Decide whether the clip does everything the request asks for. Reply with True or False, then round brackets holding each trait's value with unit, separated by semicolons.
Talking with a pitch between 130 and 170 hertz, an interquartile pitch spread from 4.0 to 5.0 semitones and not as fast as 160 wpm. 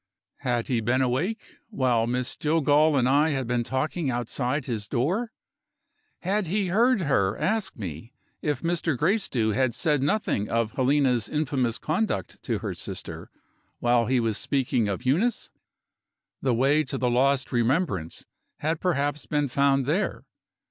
True (135 Hz; 4.5 semitones; 150 wpm)